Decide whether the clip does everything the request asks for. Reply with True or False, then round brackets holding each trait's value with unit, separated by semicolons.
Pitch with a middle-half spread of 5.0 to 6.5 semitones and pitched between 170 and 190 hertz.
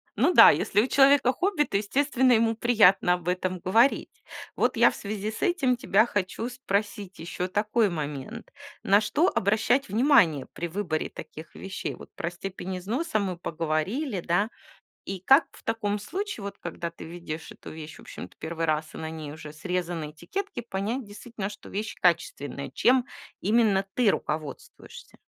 False (5.6 semitones; 200 Hz)